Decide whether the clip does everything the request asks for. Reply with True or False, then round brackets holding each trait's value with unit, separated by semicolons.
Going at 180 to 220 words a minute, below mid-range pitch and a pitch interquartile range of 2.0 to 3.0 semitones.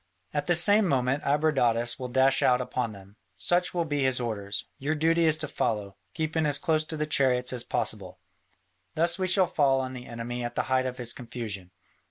False (205 wpm; 130 Hz; 4.4 semitones)